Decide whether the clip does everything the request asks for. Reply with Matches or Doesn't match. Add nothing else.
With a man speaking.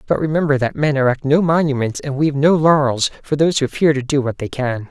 Matches